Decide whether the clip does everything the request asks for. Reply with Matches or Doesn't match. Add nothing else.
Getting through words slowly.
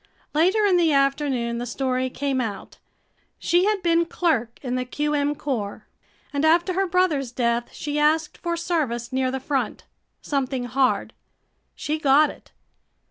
Doesn't match